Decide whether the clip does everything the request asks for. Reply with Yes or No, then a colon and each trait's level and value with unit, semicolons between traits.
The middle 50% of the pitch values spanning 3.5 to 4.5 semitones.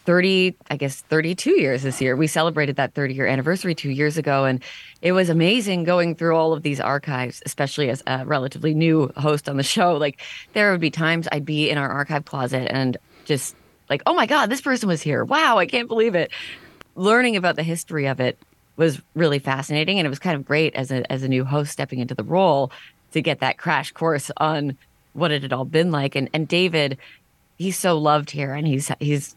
Yes: average, 3.8 semitones